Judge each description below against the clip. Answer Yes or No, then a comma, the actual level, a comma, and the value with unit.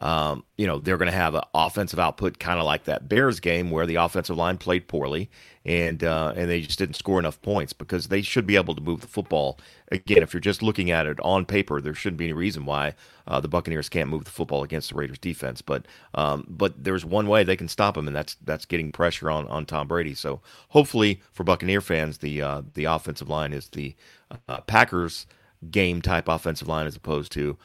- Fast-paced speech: Yes, fast, 230 wpm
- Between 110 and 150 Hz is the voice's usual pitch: No, very low, 85 Hz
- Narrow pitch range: No, average, 3.7 semitones